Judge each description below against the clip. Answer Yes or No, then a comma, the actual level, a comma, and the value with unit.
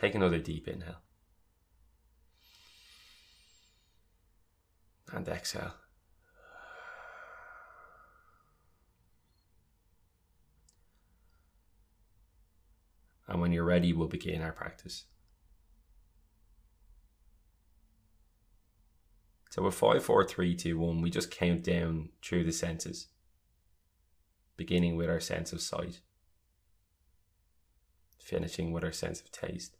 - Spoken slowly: Yes, slow, 80 wpm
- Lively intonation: No, average, 2.9 semitones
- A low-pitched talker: Yes, very low, 85 Hz